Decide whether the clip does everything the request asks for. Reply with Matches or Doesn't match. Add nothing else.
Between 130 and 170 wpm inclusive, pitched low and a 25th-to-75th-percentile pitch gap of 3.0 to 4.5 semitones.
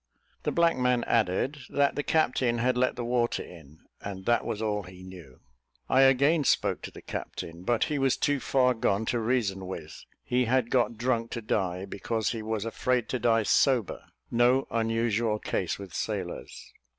Doesn't match